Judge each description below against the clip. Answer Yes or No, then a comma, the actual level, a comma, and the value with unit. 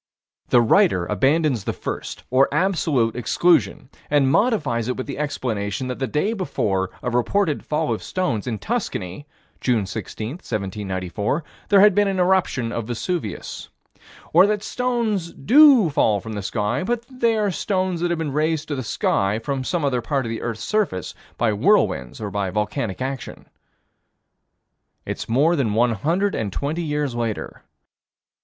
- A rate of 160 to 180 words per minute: Yes, average, 165 wpm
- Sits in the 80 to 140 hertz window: Yes, low, 135 Hz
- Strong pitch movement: Yes, wide, 8.3 semitones